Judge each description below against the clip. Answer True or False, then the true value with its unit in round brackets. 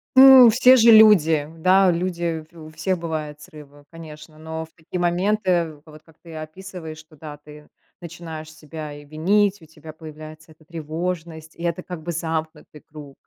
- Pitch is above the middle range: False (160 Hz)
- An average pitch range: False (2.3 semitones)